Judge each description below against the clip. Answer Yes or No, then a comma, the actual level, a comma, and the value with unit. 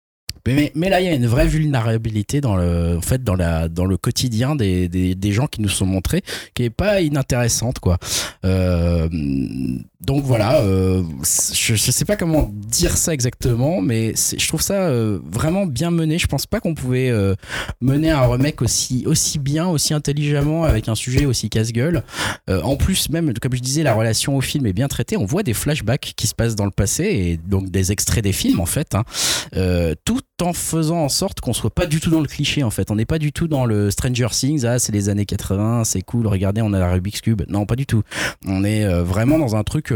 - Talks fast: Yes, fast, 230 wpm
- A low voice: Yes, low, 115 Hz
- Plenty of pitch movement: Yes, wide, 6.7 semitones